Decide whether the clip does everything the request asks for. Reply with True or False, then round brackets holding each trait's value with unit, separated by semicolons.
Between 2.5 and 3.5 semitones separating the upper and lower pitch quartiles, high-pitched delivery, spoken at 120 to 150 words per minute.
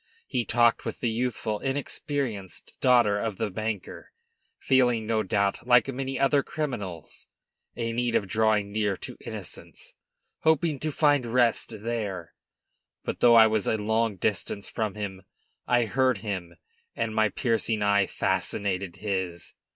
False (3.2 semitones; 110 Hz; 145 wpm)